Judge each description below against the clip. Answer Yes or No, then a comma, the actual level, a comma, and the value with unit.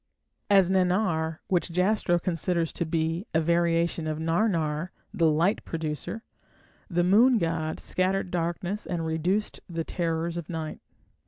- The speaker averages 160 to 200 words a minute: No, slow, 135 wpm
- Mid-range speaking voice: Yes, medium, 170 Hz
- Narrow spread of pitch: Yes, narrow, 2.2 semitones